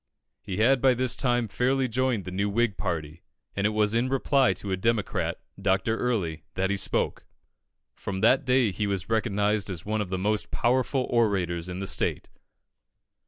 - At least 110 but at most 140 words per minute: No, average, 180 wpm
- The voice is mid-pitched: No, low, 105 Hz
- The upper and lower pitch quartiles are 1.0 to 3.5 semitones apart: No, average, 4.2 semitones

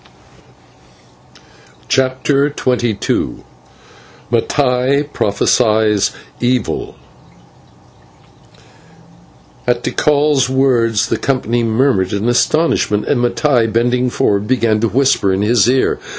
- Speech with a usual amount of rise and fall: Yes, average, 3.3 semitones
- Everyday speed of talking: No, slow, 85 wpm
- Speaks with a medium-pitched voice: No, low, 120 Hz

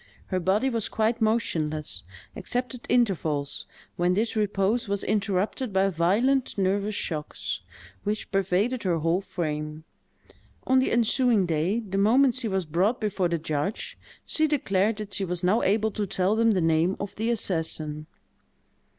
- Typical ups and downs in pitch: Yes, average, 4.4 semitones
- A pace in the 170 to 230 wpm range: No, average, 155 wpm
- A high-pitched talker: Yes, high, 195 Hz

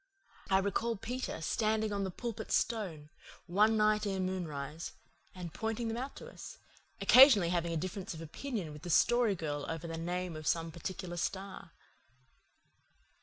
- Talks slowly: No, average, 160 wpm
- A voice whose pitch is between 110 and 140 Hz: No, high, 190 Hz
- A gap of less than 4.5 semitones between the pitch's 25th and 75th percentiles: No, average, 4.8 semitones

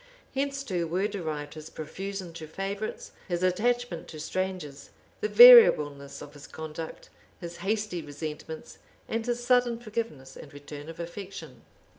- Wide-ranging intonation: Yes, wide, 5.8 semitones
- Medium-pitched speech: Yes, medium, 180 Hz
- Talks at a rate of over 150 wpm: No, average, 140 wpm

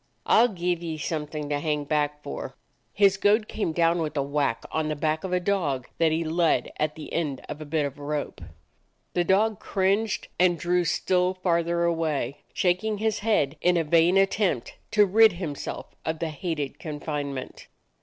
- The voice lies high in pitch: No, medium, 165 Hz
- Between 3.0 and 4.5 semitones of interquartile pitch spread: Yes, average, 3.6 semitones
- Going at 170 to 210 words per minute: Yes, average, 185 wpm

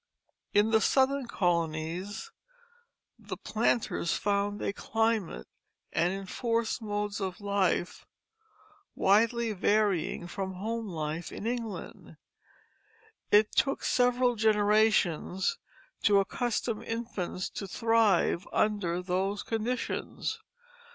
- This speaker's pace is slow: Yes, slow, 95 wpm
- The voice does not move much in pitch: No, average, 3.4 semitones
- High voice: Yes, high, 210 Hz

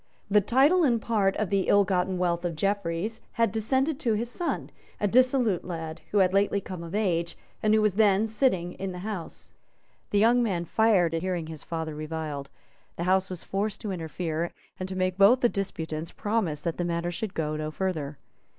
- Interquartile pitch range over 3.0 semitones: Yes, average, 4.2 semitones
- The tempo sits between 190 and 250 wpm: Yes, average, 200 wpm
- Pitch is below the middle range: No, high, 190 Hz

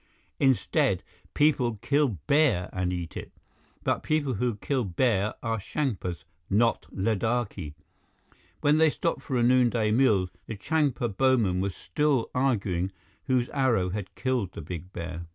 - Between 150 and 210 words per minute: No, average, 140 wpm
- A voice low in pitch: Yes, low, 115 Hz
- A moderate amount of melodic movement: No, wide, 5.7 semitones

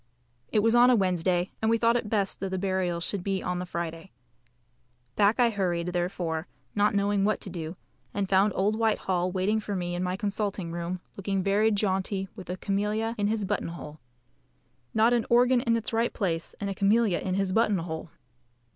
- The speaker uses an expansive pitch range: No, average, 3.0 semitones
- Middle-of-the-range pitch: No, high, 195 Hz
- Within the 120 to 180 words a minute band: No, average, 200 wpm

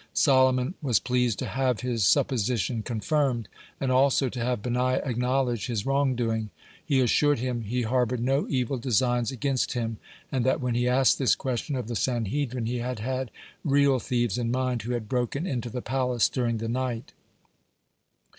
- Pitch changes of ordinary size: No, narrow, 1.9 semitones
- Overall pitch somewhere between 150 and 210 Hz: No, low, 125 Hz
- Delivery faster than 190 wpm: No, average, 175 wpm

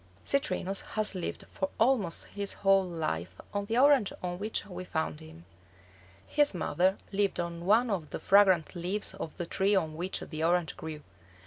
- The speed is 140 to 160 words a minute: No, average, 175 wpm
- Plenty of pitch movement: No, average, 3.3 semitones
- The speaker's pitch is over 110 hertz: Yes, medium, 185 Hz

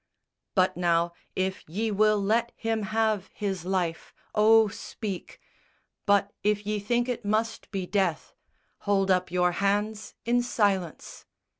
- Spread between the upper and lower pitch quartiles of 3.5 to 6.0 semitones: No, narrow, 2.5 semitones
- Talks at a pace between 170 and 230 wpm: No, slow, 135 wpm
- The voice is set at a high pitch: Yes, high, 205 Hz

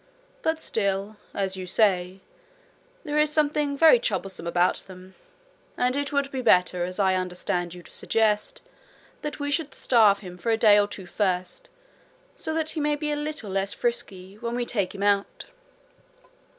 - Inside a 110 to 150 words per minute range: No, average, 175 wpm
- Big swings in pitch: Yes, wide, 7.3 semitones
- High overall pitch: Yes, high, 210 Hz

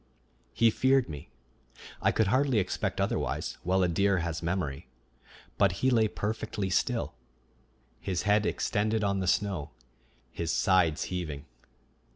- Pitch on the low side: Yes, very low, 95 Hz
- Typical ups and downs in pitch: Yes, average, 4.1 semitones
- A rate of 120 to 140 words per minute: Yes, slow, 135 wpm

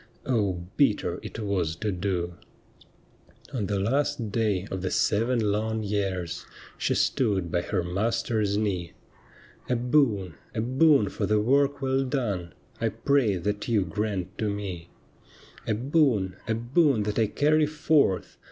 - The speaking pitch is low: Yes, low, 105 Hz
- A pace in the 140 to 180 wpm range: Yes, average, 155 wpm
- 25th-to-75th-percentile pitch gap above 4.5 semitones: Yes, average, 4.9 semitones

